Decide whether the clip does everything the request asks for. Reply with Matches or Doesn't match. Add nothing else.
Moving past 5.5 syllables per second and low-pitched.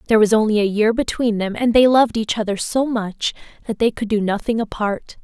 Doesn't match